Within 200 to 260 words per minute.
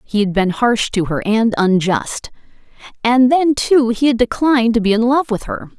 Yes: fast, 205 wpm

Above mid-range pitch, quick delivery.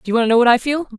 Yes: high, 240 Hz; fast, 485 wpm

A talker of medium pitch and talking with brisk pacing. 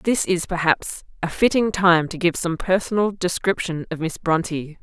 No: medium, 175 Hz; average, 175 wpm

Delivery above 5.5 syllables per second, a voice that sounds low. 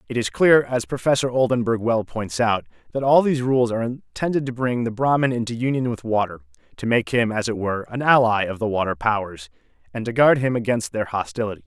Yes: 5.9 syllables/s; low, 115 Hz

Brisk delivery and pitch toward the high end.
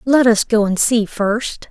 Yes: fast, 210 wpm; high, 225 Hz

